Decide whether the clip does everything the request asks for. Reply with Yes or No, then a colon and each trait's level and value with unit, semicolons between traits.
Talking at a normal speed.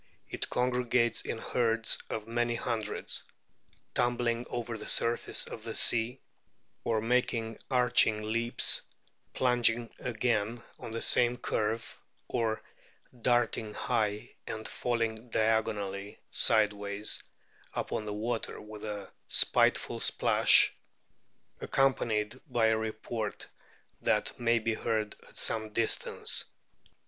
No: slow, 110 wpm